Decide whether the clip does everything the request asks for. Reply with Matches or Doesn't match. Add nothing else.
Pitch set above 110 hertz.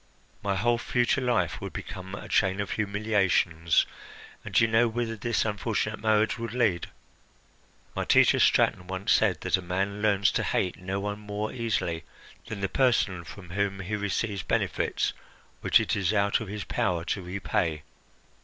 Doesn't match